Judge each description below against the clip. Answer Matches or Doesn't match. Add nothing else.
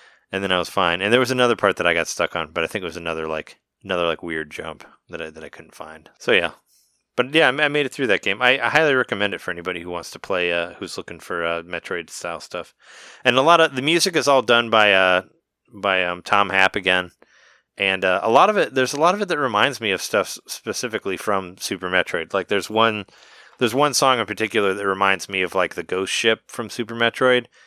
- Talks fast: Matches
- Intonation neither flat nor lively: Doesn't match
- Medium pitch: Doesn't match